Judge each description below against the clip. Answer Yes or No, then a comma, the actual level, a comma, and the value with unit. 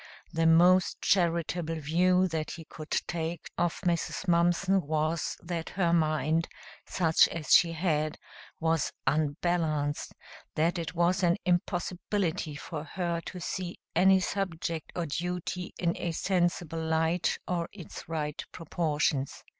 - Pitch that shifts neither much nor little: No, narrow, 1.9 semitones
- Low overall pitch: No, medium, 170 Hz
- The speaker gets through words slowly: Yes, slow, 130 wpm